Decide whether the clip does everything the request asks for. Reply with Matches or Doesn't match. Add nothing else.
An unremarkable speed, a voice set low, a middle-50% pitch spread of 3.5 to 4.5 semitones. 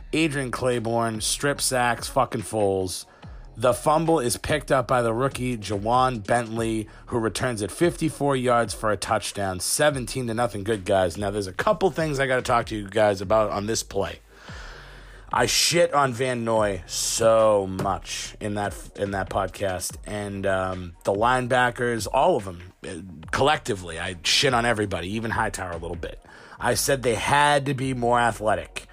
Matches